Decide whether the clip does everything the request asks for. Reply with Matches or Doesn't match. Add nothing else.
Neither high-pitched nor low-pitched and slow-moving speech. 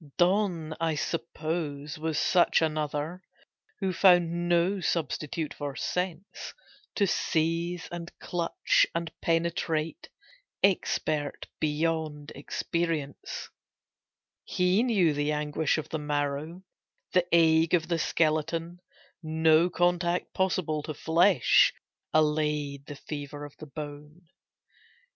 Matches